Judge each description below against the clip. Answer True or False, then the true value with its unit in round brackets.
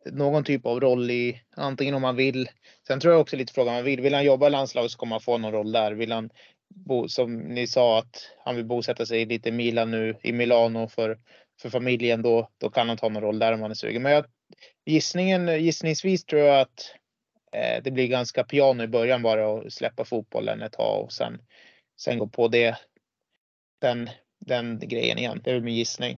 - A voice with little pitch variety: False (3.2 semitones)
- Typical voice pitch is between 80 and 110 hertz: False (120 Hz)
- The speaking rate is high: True (220 wpm)